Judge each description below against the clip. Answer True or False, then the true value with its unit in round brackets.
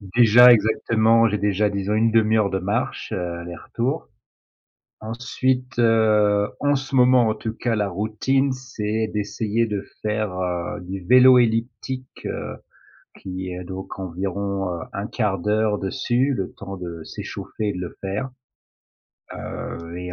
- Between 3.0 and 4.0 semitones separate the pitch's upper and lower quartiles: True (3.4 semitones)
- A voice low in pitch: True (105 Hz)